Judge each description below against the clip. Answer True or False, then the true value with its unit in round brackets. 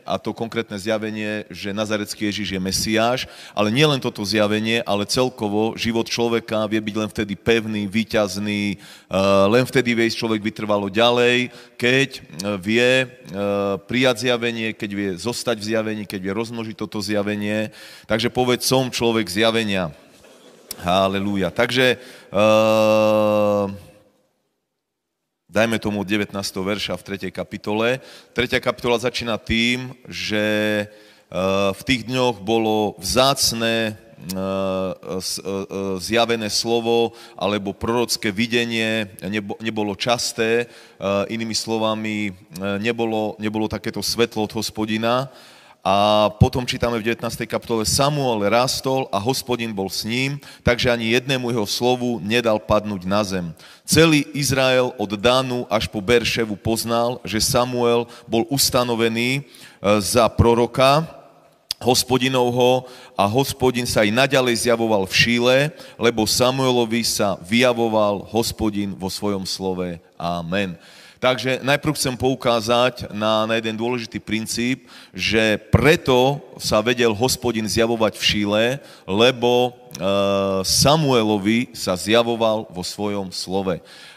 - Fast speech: False (115 wpm)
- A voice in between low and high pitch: False (110 Hz)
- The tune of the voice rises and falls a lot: False (2.7 semitones)